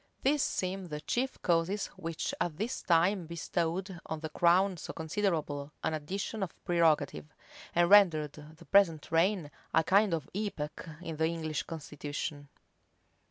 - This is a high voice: No, medium, 165 Hz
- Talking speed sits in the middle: Yes, average, 145 wpm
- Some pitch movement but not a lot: Yes, average, 3.7 semitones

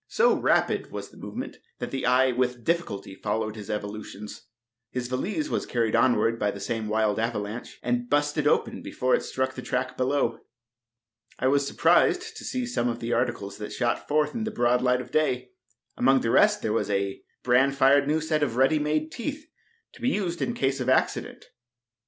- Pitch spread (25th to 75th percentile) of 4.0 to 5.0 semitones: Yes, average, 4.3 semitones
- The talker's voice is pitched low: Yes, low, 125 Hz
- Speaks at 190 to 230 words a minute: Yes, average, 195 wpm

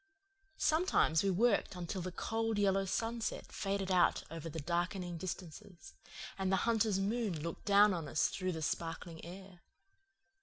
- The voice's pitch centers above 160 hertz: Yes, medium, 185 Hz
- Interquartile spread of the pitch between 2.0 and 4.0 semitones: Yes, average, 3.0 semitones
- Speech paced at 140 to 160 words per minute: Yes, average, 150 wpm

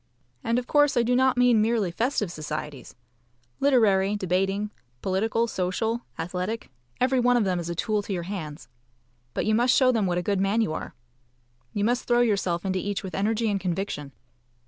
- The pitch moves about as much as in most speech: Yes, average, 4.2 semitones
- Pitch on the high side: Yes, high, 205 Hz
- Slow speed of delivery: No, average, 190 wpm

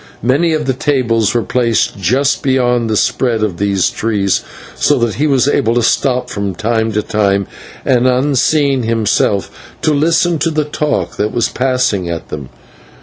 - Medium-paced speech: Yes, average, 170 wpm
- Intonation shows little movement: No, average, 4.5 semitones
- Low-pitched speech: Yes, low, 120 Hz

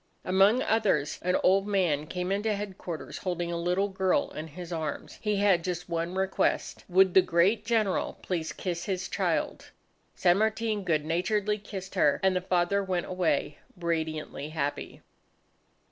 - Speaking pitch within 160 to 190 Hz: Yes, medium, 185 Hz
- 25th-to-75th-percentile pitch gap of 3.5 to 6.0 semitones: No, average, 2.8 semitones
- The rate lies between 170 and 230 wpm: No, average, 155 wpm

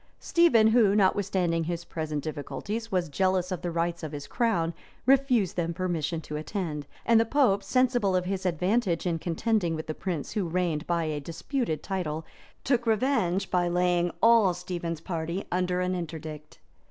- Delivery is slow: No, average, 165 wpm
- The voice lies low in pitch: No, medium, 180 Hz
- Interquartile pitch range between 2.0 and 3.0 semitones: No, average, 3.7 semitones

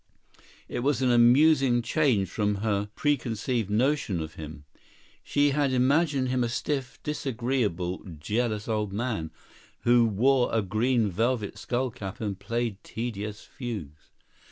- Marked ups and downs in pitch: No, average, 3.9 semitones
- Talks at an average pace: No, slow, 130 wpm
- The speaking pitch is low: Yes, low, 120 Hz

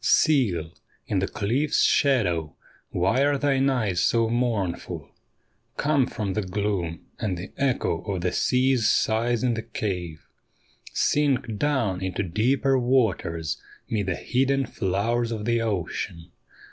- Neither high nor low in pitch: No, low, 110 Hz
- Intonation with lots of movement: Yes, wide, 5.7 semitones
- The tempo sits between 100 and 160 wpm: Yes, slow, 135 wpm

